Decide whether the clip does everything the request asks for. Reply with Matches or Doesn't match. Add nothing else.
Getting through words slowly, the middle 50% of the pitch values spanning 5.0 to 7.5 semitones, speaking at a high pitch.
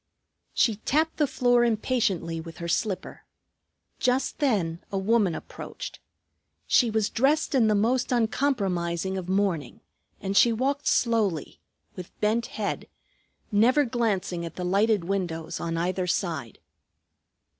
Matches